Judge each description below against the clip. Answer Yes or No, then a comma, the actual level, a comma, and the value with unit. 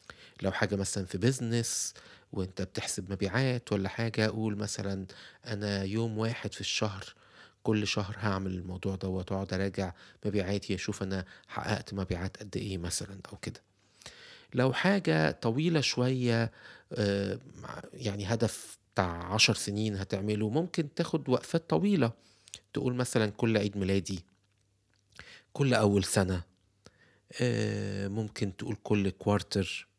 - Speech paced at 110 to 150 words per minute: Yes, average, 120 wpm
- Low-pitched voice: Yes, low, 105 Hz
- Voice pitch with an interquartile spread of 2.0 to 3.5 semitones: Yes, average, 2.8 semitones